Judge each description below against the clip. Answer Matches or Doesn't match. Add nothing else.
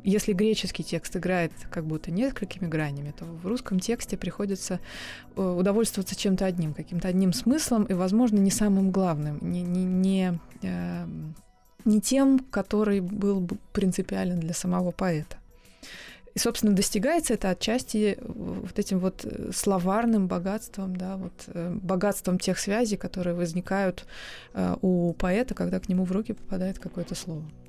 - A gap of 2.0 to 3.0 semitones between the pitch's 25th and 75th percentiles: Matches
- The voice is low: Doesn't match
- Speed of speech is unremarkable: Matches